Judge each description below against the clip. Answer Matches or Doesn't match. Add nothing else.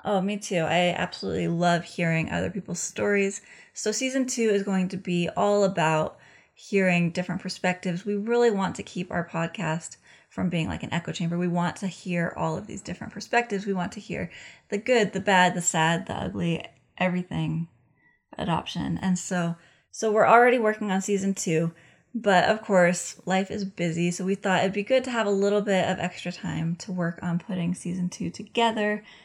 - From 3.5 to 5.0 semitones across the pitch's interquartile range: Doesn't match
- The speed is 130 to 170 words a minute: Doesn't match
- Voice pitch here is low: Doesn't match